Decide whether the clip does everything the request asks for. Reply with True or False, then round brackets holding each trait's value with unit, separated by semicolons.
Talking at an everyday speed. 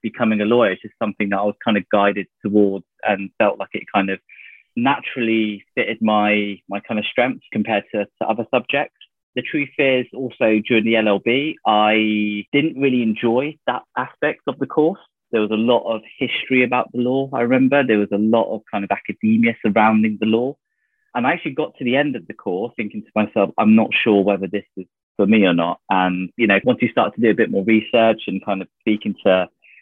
False (220 wpm)